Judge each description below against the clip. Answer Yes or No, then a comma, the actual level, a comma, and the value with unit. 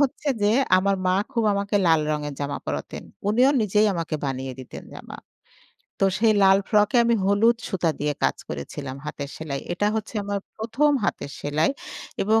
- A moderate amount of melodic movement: No, wide, 6.6 semitones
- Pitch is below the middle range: No, high, 195 Hz